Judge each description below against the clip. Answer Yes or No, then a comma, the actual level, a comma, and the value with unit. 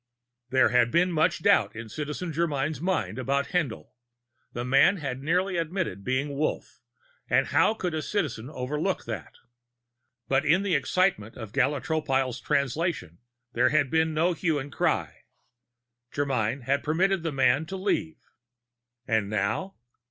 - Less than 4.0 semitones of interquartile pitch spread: No, average, 4.8 semitones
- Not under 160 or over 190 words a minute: No, average, 145 wpm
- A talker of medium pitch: Yes, medium, 145 Hz